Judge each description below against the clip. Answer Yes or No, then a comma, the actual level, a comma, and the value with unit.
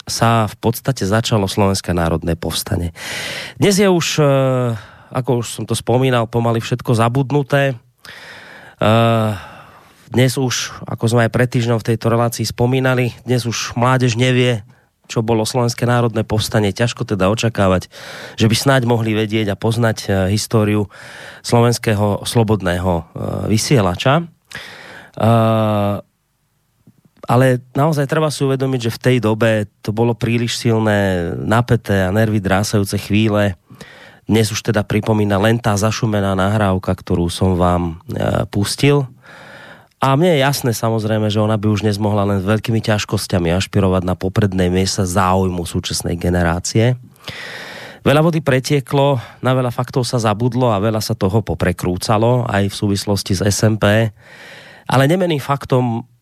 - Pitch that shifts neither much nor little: Yes, average, 3.4 semitones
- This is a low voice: Yes, low, 115 Hz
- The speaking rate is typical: Yes, average, 130 wpm